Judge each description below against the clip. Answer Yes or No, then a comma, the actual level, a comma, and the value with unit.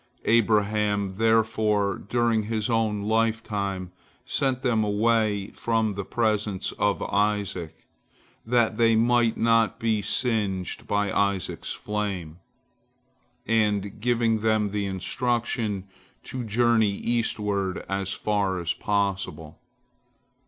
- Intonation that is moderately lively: No, narrow, 2.1 semitones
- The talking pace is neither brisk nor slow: No, slow, 105 wpm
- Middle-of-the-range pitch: No, low, 105 Hz